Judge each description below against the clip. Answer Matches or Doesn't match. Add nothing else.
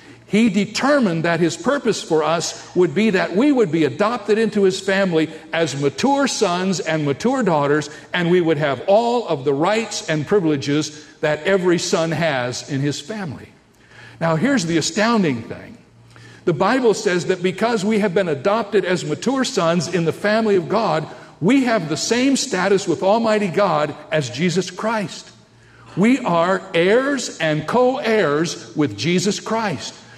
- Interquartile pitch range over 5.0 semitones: Matches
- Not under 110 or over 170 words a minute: Matches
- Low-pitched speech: Doesn't match